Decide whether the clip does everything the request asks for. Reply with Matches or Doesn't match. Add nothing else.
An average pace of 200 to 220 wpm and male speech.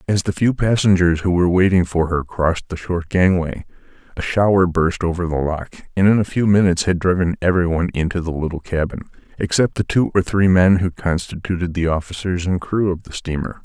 Matches